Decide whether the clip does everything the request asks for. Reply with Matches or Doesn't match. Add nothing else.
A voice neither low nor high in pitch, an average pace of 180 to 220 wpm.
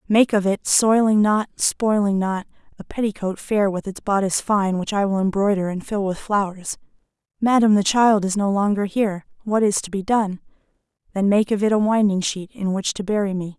Doesn't match